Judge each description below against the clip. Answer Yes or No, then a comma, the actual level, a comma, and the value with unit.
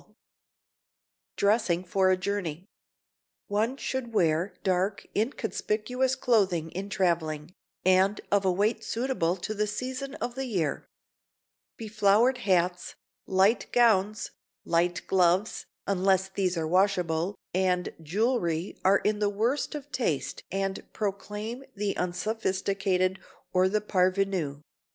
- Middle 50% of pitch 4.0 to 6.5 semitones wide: No, average, 2.9 semitones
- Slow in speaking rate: Yes, slow, 115 wpm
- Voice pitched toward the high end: Yes, high, 195 Hz